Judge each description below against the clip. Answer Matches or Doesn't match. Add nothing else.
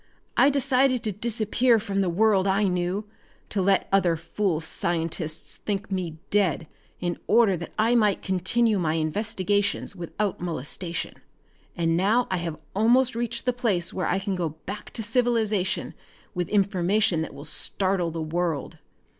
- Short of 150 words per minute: Doesn't match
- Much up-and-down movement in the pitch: Doesn't match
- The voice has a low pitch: Doesn't match